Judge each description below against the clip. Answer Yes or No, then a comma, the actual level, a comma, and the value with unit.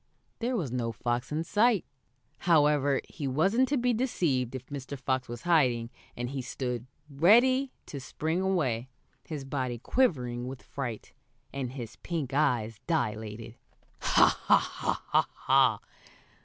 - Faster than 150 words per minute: No, slow, 135 wpm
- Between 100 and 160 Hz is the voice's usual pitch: Yes, low, 135 Hz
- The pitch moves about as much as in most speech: No, wide, 5.7 semitones